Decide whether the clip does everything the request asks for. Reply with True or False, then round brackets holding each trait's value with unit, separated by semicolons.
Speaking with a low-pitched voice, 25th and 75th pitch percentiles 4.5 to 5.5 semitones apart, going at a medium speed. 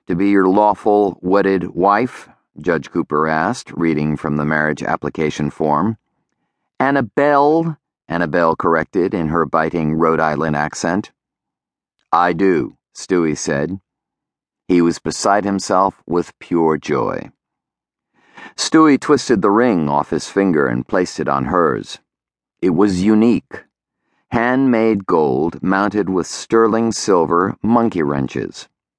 False (90 Hz; 5.2 semitones; 120 wpm)